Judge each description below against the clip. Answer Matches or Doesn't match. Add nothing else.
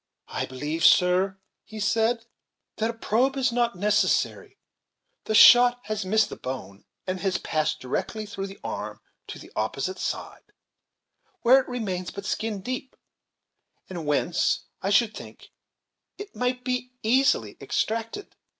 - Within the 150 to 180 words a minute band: Doesn't match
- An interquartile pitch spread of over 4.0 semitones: Matches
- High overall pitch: Matches